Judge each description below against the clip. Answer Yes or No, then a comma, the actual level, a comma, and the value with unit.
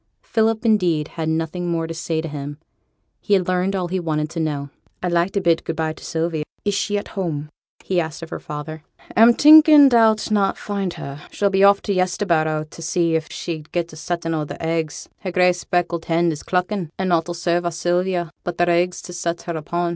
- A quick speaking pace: Yes, fast, 225 wpm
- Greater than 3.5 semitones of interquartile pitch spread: No, narrow, 2.6 semitones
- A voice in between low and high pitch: Yes, medium, 175 Hz